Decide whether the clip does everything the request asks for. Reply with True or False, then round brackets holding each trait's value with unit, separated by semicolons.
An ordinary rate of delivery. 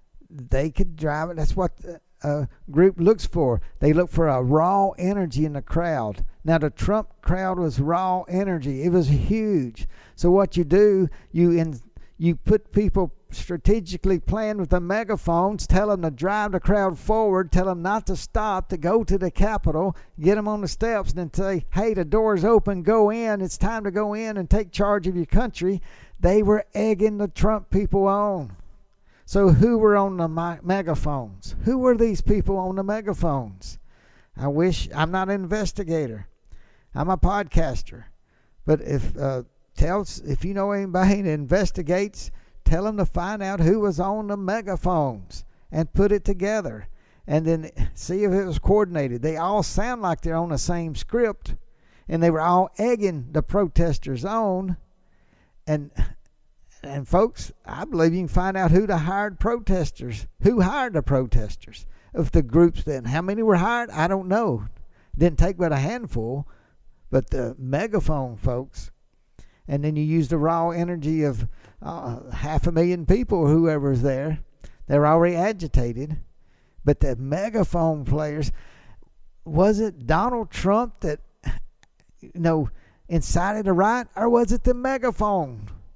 True (165 wpm)